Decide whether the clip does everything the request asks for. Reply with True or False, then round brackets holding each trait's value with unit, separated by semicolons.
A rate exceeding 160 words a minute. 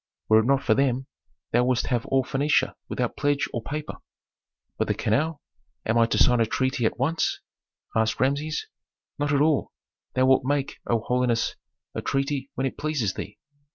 True (180 wpm)